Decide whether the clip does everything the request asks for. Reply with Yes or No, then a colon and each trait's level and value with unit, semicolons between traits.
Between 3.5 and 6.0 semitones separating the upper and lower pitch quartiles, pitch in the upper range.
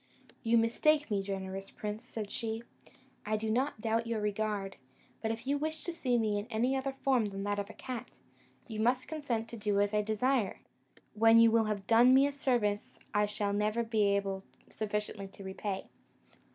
No: average, 2.7 semitones; high, 220 Hz